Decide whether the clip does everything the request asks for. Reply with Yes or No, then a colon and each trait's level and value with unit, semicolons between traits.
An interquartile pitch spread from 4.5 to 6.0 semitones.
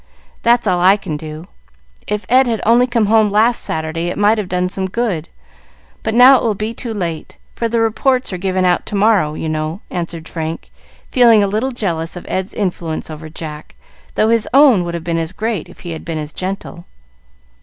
Yes: average, 5.3 semitones